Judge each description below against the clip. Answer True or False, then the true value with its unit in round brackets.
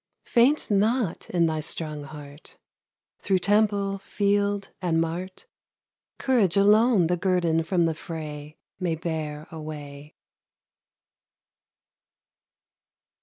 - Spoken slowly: True (95 wpm)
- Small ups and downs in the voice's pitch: False (4.3 semitones)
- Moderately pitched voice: True (175 Hz)